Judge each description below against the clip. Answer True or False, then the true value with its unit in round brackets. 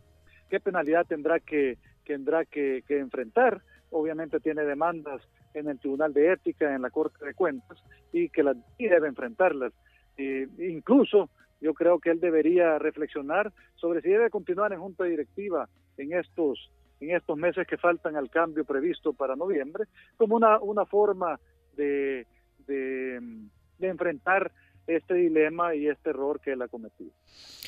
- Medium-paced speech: True (155 wpm)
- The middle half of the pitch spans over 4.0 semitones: True (4.5 semitones)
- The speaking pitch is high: False (155 Hz)